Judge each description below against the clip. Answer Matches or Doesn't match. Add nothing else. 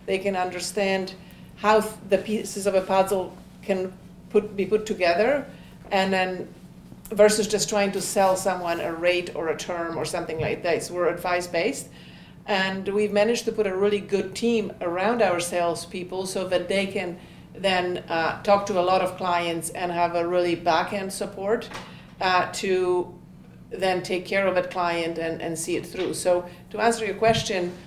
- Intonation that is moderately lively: Doesn't match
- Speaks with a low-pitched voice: Doesn't match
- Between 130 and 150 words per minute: Doesn't match